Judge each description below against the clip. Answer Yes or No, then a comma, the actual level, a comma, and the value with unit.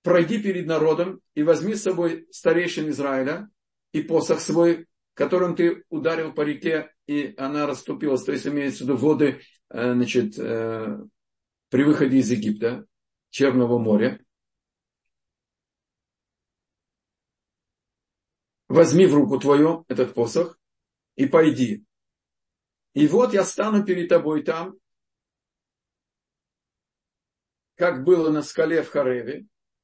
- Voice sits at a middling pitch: Yes, medium, 155 Hz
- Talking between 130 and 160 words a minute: No, slow, 110 wpm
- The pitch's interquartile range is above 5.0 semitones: No, average, 4.3 semitones